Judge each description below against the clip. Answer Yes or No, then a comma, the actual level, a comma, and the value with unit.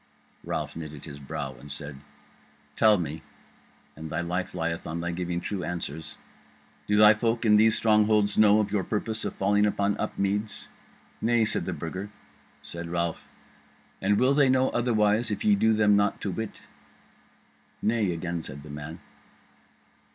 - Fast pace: No, average, 160 wpm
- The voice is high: No, low, 100 Hz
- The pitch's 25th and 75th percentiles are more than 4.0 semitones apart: Yes, average, 4.5 semitones